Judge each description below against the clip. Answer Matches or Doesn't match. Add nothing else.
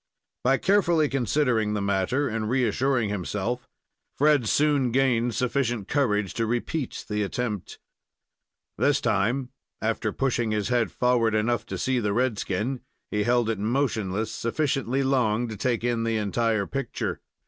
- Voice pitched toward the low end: Matches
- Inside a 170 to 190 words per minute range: Doesn't match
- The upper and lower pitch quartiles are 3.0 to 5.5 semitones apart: Matches